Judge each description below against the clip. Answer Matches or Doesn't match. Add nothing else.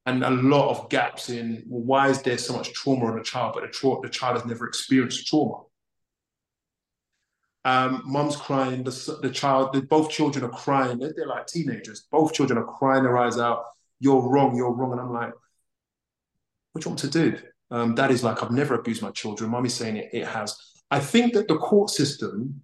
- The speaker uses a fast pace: Matches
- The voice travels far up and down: Doesn't match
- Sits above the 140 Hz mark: Doesn't match